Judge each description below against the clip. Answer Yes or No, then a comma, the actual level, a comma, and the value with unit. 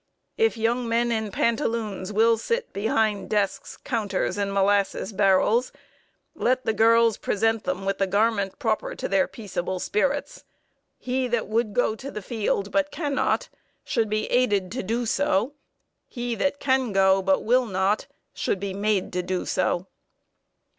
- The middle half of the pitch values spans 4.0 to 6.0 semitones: No, average, 3.4 semitones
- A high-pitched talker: Yes, high, 220 Hz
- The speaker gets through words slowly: No, average, 155 wpm